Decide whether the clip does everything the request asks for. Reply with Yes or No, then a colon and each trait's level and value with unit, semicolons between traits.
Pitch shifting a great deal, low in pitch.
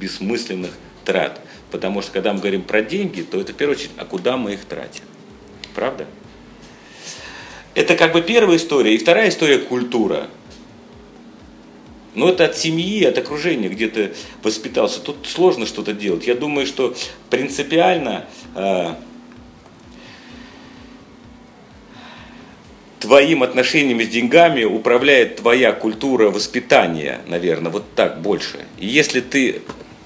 Yes: wide, 7.2 semitones; low, 125 Hz